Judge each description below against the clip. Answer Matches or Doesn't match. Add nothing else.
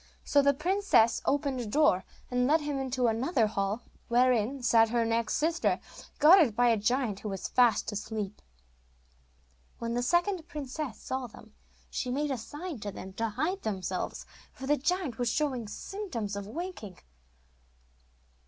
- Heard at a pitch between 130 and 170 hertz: Doesn't match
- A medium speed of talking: Matches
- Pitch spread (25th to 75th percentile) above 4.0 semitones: Matches